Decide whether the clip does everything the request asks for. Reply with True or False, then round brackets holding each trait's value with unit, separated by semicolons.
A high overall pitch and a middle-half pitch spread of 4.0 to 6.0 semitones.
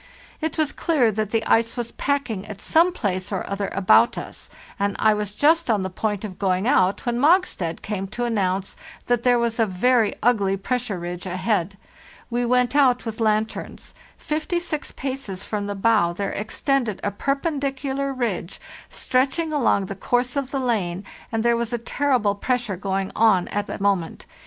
True (225 Hz; 4.6 semitones)